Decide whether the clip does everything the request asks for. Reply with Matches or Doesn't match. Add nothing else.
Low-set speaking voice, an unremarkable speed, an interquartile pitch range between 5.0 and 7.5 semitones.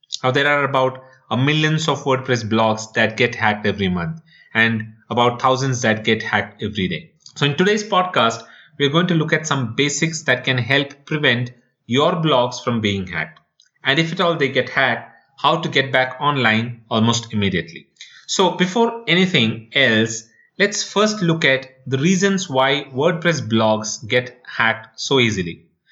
Matches